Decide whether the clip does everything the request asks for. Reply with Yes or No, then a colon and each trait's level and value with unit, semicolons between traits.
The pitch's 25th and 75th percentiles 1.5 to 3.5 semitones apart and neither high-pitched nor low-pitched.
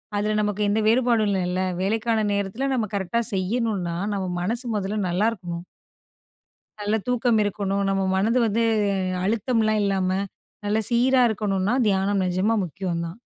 No: average, 2.9 semitones; high, 205 Hz